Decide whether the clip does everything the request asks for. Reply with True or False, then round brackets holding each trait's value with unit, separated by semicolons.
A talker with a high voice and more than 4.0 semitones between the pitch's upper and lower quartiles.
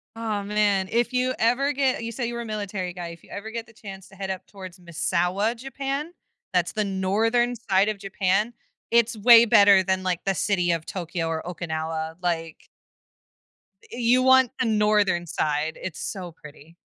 True (200 Hz; 4.6 semitones)